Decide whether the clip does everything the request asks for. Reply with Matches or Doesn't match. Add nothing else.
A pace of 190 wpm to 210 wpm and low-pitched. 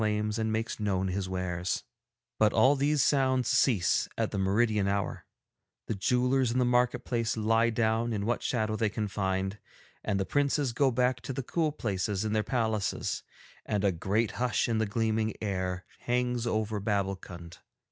Doesn't match